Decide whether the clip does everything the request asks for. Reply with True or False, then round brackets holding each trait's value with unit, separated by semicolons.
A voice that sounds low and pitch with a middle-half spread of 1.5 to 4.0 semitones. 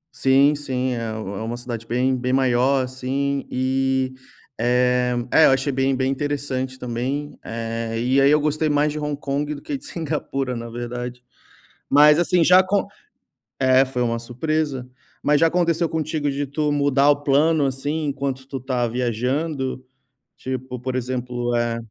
True (130 Hz; 2.8 semitones)